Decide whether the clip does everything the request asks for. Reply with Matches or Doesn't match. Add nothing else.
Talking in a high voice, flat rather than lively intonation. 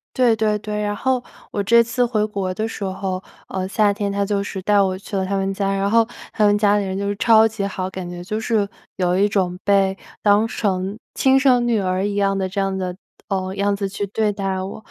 Matches